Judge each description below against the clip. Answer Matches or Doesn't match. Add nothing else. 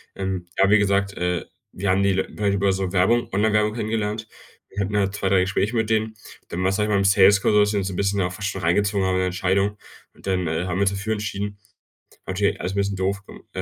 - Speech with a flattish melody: Matches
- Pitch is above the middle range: Doesn't match